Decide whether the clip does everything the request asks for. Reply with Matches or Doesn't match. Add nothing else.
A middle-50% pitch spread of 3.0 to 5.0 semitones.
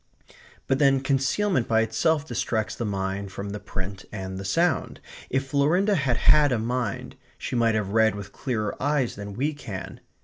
Doesn't match